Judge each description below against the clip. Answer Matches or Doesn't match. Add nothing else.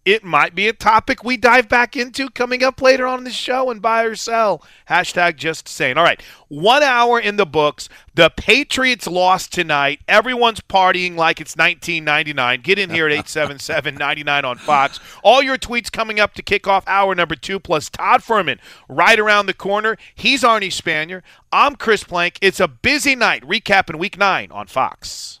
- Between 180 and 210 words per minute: Matches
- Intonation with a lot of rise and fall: Matches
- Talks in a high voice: Matches